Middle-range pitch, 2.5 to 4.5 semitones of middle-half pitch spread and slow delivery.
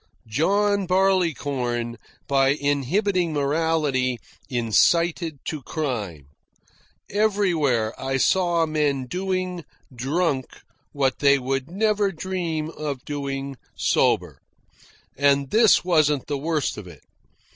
No: medium, 150 Hz; average, 4.9 semitones; slow, 100 wpm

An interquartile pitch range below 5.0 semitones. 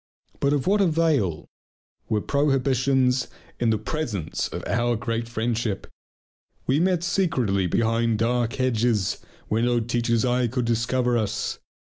Yes: average, 2.9 semitones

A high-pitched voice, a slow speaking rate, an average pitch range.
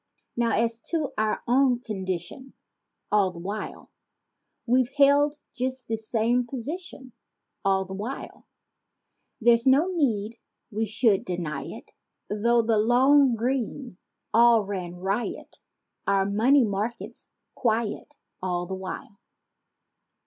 Yes: high, 230 Hz; slow, 120 wpm; average, 4.3 semitones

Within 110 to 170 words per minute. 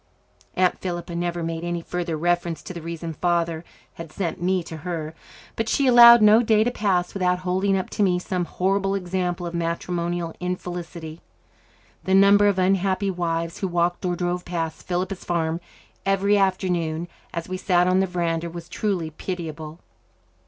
Yes: average, 165 wpm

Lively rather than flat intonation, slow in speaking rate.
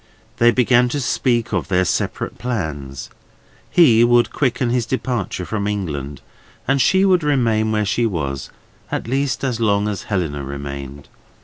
No: wide, 7.2 semitones; average, 150 wpm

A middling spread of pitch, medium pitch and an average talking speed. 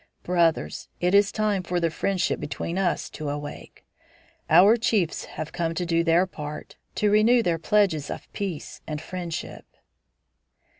Yes: average, 3.5 semitones; medium, 175 Hz; average, 150 wpm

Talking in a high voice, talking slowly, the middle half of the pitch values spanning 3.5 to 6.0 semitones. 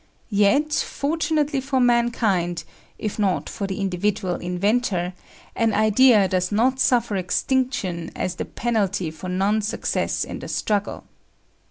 Yes: high, 210 Hz; slow, 130 wpm; average, 5.0 semitones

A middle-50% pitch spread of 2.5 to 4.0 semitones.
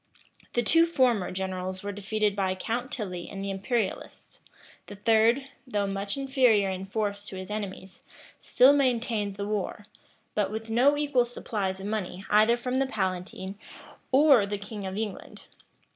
Yes: average, 3.7 semitones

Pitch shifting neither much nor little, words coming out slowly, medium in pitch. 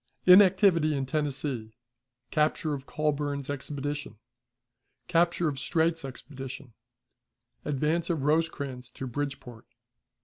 Yes: average, 3.0 semitones; slow, 95 wpm; medium, 145 Hz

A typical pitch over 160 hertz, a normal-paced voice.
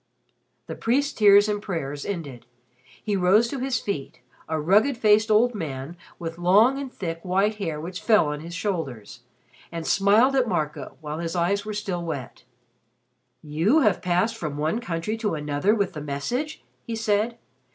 Yes: high, 190 Hz; average, 170 wpm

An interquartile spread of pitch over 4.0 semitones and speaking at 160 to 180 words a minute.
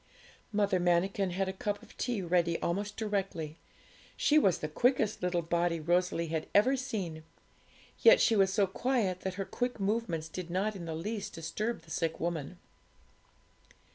No: average, 3.7 semitones; average, 165 wpm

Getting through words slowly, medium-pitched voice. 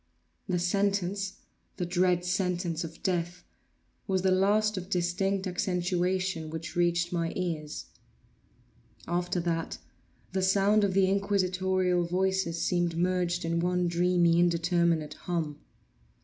Yes: slow, 110 wpm; medium, 180 Hz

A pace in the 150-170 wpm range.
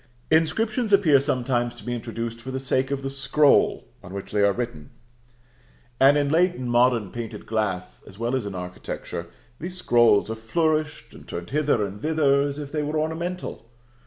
No: average, 185 wpm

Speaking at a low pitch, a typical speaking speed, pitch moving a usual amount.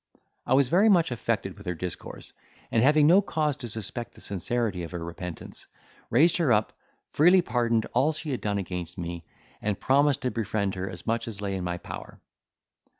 No: low, 115 Hz; average, 195 wpm; wide, 7.0 semitones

